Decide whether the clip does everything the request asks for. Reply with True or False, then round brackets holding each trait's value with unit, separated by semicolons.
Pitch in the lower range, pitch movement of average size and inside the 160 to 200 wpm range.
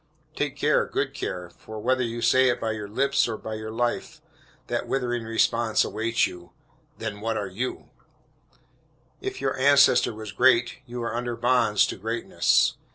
False (115 Hz; 2.2 semitones; 165 wpm)